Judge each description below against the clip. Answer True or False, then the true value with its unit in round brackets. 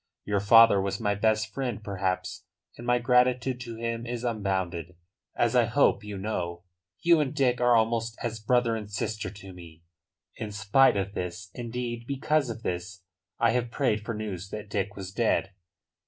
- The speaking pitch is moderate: False (110 Hz)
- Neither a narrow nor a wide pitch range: True (3.4 semitones)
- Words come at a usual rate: True (175 wpm)